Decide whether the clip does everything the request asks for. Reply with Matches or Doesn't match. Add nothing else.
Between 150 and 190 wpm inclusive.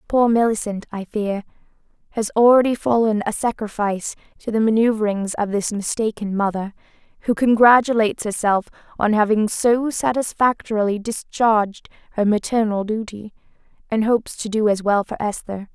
Doesn't match